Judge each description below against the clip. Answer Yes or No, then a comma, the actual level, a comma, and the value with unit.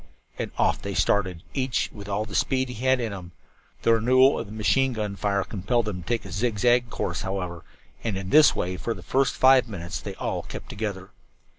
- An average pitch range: Yes, average, 4.2 semitones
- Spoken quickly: Yes, fast, 220 wpm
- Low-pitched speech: Yes, low, 110 Hz